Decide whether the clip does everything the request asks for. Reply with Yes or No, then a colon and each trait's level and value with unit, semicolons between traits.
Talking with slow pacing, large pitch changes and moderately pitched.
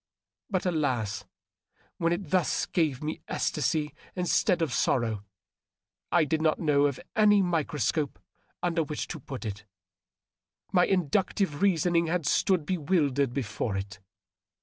No: slow, 125 wpm; average, 4.1 semitones; medium, 155 Hz